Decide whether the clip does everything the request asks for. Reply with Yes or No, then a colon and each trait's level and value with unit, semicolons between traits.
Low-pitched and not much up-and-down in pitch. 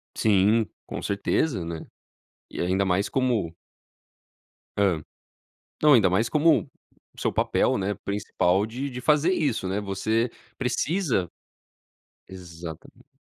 No: low, 105 Hz; average, 5.2 semitones